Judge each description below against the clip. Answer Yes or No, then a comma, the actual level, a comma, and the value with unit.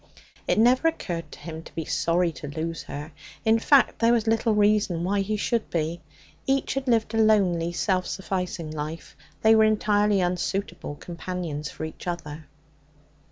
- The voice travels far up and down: No, average, 4.7 semitones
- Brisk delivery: No, average, 165 wpm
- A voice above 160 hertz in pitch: Yes, medium, 185 Hz